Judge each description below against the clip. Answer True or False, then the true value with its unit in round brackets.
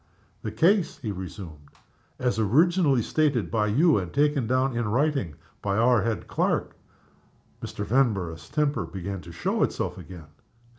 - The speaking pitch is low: True (115 Hz)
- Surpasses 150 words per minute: False (145 wpm)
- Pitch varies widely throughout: True (6.5 semitones)